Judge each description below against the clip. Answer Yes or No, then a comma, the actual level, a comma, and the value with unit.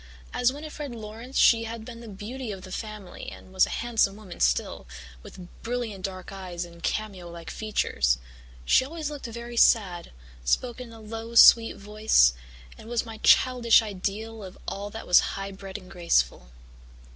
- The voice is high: Yes, high, 215 Hz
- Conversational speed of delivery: Yes, average, 170 wpm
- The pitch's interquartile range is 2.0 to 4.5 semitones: Yes, average, 3.8 semitones